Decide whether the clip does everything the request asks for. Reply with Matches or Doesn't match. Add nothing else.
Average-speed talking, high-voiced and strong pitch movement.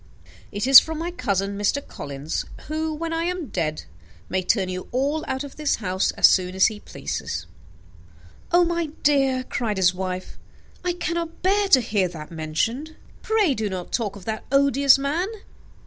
Matches